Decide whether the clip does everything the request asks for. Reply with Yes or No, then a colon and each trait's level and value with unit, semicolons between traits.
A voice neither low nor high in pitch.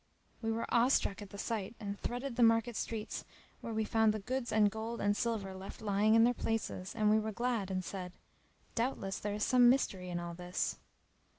No: high, 220 Hz